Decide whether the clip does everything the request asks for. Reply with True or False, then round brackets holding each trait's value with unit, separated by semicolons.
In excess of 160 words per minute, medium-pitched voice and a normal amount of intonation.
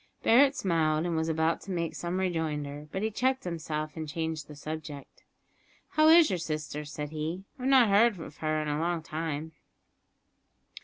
True (185 wpm; 160 Hz; 3.6 semitones)